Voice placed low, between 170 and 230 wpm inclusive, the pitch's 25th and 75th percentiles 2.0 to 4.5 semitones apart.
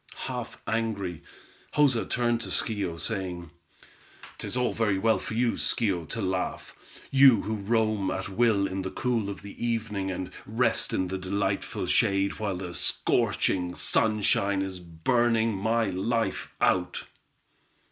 No: low, 100 Hz; average, 140 wpm; average, 3.3 semitones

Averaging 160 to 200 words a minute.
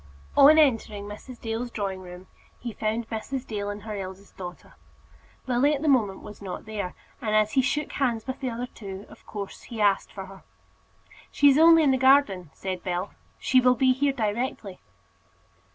Yes: average, 185 wpm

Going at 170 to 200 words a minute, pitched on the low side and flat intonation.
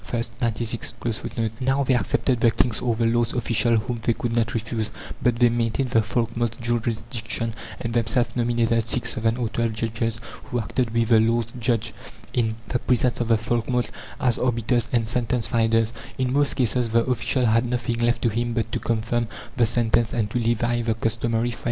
Yes: average, 185 wpm; low, 115 Hz; narrow, 1.1 semitones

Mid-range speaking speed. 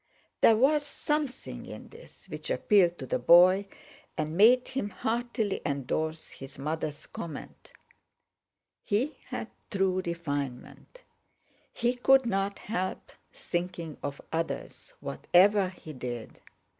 No: slow, 110 wpm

